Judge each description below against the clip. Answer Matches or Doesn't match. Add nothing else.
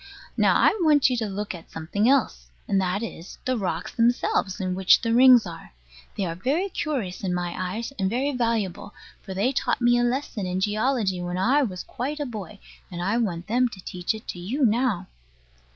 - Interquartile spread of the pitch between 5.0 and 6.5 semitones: Matches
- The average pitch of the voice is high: Matches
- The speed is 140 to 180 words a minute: Doesn't match